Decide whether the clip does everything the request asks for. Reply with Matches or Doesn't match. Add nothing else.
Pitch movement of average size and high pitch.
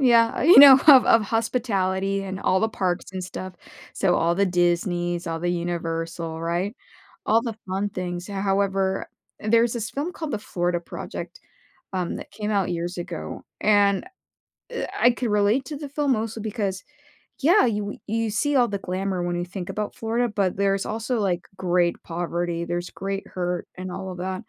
Matches